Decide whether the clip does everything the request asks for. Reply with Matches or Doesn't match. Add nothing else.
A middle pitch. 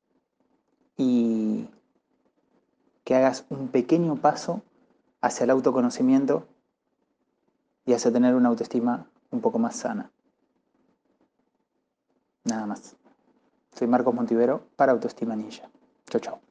Matches